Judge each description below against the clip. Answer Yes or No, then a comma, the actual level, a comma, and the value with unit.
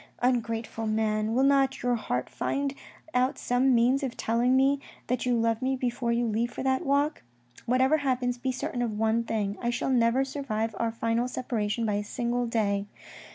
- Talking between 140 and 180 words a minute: No, average, 190 wpm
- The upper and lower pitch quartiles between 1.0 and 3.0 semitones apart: Yes, narrow, 2.5 semitones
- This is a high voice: Yes, high, 240 Hz